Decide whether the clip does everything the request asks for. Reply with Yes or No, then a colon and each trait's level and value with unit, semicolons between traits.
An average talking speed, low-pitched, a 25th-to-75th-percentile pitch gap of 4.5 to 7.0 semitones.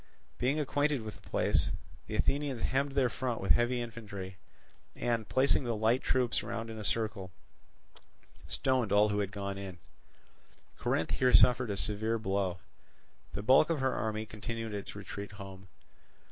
No: average, 160 wpm; low, 110 Hz; average, 3.7 semitones